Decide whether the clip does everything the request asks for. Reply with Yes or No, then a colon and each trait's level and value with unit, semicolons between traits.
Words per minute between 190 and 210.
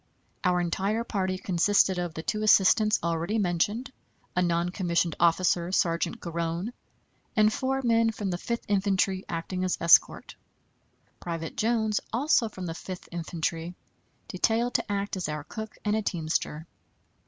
No: average, 145 wpm